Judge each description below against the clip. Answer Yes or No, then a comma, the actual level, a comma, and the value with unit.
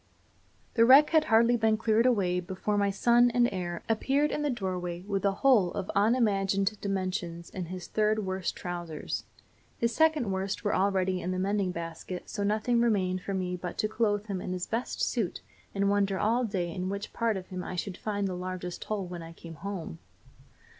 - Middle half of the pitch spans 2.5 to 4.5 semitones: Yes, average, 3.3 semitones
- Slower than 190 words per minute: No, average, 195 wpm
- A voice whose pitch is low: No, high, 195 Hz